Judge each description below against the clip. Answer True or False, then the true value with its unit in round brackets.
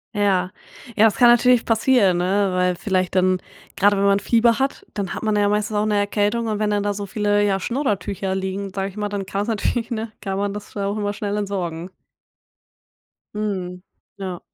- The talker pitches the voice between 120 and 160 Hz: False (205 Hz)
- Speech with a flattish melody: True (1.8 semitones)